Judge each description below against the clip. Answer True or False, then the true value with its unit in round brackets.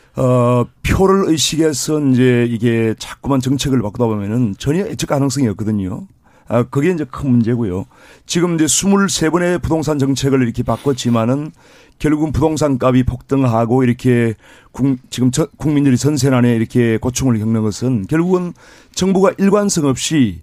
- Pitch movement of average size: True (4.4 semitones)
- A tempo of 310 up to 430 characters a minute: True (330 characters per minute)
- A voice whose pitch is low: True (130 Hz)